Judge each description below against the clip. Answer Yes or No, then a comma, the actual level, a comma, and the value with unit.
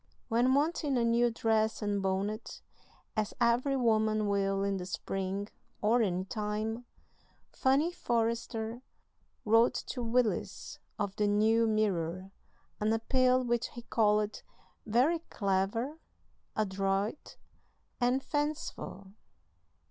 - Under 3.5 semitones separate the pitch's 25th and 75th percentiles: Yes, average, 3.0 semitones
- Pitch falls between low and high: No, high, 220 Hz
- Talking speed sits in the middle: No, slow, 110 wpm